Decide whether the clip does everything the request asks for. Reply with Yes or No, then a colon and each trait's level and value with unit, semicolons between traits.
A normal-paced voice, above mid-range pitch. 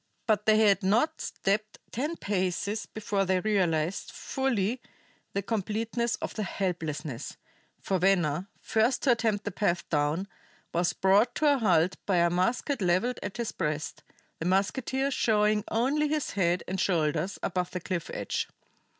Yes: average, 150 wpm; high, 200 Hz